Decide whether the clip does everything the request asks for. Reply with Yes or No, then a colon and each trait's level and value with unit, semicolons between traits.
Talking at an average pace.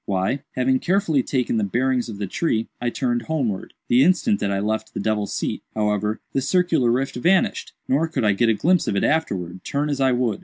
No: fast, 220 wpm